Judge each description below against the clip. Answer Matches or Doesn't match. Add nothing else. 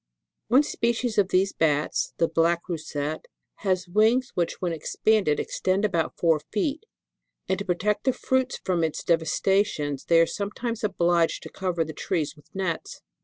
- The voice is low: Doesn't match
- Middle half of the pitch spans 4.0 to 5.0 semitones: Matches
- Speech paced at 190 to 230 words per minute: Doesn't match